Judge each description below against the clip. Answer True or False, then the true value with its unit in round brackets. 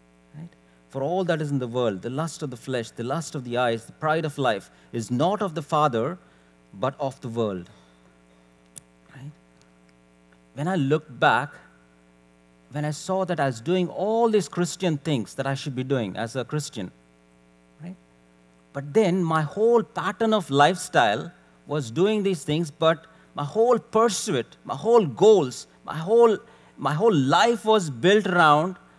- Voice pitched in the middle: True (145 Hz)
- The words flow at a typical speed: True (170 wpm)